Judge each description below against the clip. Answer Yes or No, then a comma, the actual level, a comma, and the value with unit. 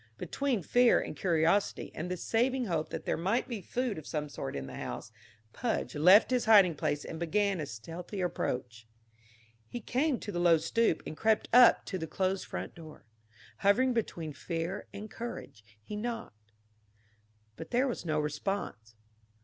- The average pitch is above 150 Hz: Yes, medium, 185 Hz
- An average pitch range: No, wide, 6.6 semitones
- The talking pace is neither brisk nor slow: Yes, average, 170 wpm